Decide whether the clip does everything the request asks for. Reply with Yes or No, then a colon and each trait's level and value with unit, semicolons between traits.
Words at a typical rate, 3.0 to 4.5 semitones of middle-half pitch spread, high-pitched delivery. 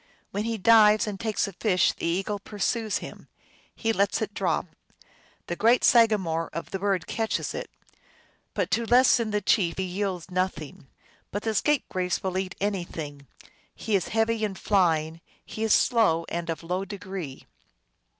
Yes: average, 170 wpm; average, 3.7 semitones; high, 195 Hz